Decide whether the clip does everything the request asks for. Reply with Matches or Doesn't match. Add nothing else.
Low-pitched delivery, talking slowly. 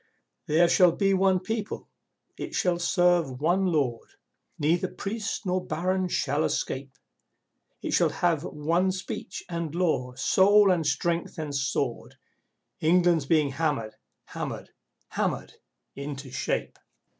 Doesn't match